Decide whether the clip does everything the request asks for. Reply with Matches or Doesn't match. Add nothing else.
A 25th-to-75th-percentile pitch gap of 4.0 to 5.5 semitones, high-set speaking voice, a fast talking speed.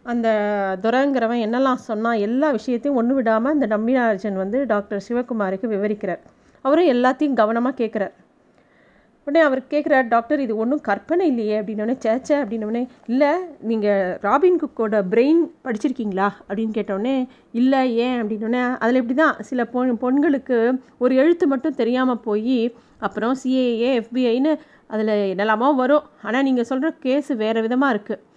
Doesn't match